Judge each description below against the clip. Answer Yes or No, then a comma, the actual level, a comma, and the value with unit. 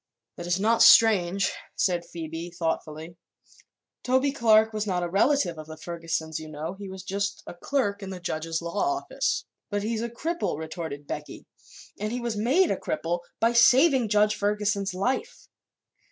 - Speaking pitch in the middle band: No, high, 200 Hz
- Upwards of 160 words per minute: Yes, average, 170 wpm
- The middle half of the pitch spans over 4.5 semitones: Yes, average, 5.2 semitones